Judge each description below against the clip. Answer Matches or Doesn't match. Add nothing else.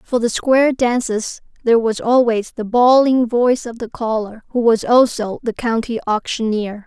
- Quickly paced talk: Doesn't match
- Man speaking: Doesn't match